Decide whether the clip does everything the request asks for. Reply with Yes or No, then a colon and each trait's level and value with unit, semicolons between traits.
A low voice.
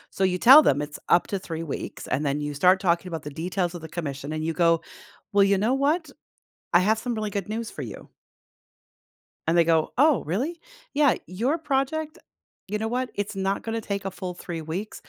No: high, 190 Hz